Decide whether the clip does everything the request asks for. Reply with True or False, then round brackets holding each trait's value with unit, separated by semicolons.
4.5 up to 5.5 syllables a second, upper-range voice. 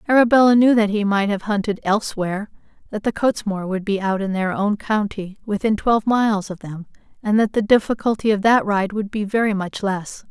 False (5.7 syllables/s; 205 Hz)